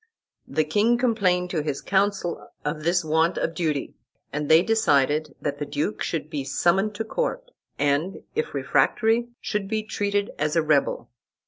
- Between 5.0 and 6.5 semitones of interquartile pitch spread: Yes, wide, 5.5 semitones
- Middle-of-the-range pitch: Yes, medium, 170 Hz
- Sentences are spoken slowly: No, average, 160 wpm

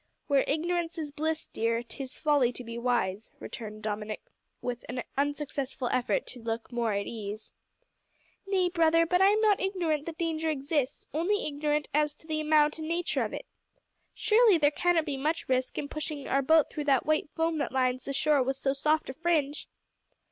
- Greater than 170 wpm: Yes, average, 190 wpm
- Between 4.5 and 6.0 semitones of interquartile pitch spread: No, average, 4.0 semitones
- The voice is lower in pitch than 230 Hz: No, very high, 295 Hz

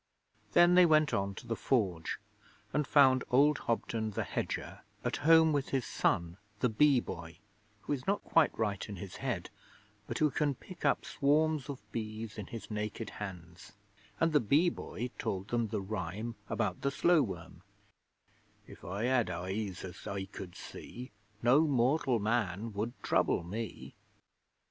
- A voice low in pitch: Yes, low, 115 Hz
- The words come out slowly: No, average, 165 wpm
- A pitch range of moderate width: No, wide, 6.3 semitones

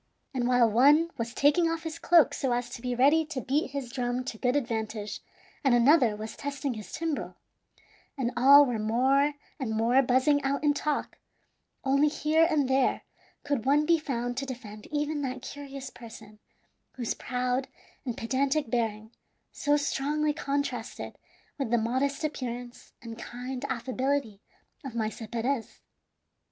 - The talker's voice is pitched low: No, very high, 260 Hz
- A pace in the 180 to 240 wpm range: No, average, 155 wpm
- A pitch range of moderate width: Yes, average, 3.3 semitones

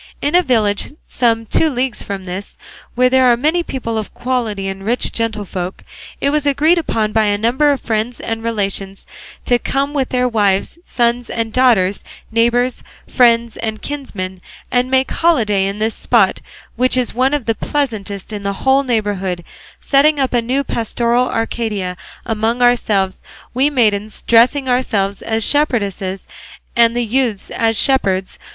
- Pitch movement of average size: Yes, average, 3.8 semitones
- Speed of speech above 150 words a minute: Yes, average, 160 wpm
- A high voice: Yes, high, 230 Hz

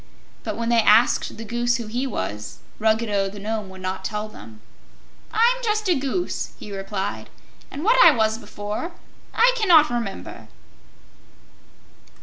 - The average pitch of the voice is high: Yes, high, 225 Hz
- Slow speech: No, average, 145 wpm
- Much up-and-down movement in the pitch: Yes, wide, 6.9 semitones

